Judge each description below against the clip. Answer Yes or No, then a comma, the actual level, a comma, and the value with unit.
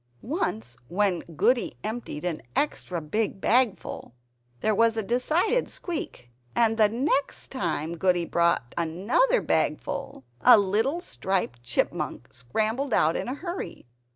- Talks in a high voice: Yes, high, 215 Hz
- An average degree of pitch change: No, wide, 7.2 semitones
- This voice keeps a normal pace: No, slow, 125 wpm